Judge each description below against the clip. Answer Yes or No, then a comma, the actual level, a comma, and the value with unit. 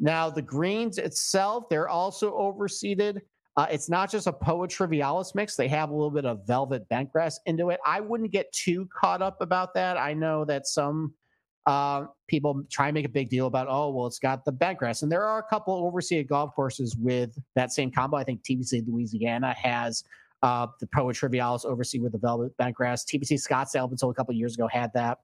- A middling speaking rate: No, fast, 210 wpm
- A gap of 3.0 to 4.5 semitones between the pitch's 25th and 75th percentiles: No, wide, 5.5 semitones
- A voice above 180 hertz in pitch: No, medium, 145 Hz